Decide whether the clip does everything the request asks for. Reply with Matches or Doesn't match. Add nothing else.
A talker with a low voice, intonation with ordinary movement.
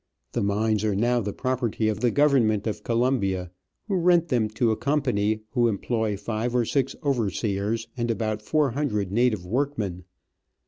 Matches